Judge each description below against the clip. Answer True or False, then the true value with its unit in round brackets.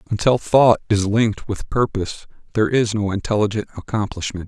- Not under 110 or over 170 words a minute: True (145 wpm)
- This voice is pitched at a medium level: False (105 Hz)